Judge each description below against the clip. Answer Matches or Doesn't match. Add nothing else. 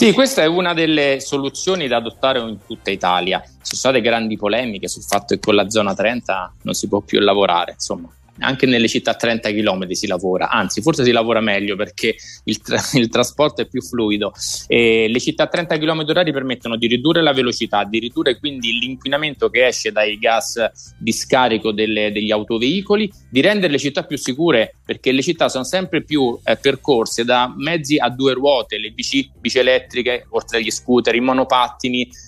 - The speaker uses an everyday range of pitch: Matches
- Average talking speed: Doesn't match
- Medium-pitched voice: Doesn't match